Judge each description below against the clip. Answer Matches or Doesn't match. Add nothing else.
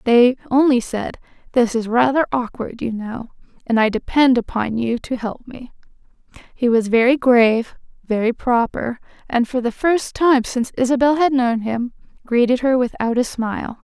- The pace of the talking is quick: Doesn't match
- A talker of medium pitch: Doesn't match